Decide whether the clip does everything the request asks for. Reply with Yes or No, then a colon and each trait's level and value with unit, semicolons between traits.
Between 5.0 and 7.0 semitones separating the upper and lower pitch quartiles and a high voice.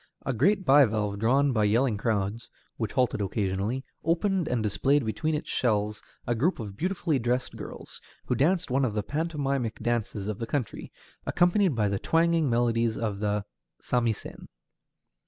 No: wide, 5.4 semitones; low, 120 Hz